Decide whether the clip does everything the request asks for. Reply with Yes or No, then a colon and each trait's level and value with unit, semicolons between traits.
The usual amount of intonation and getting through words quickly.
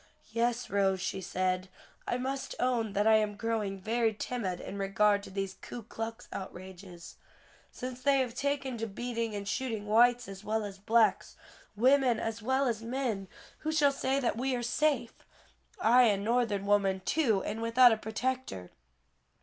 No: average, 3.7 semitones; average, 165 wpm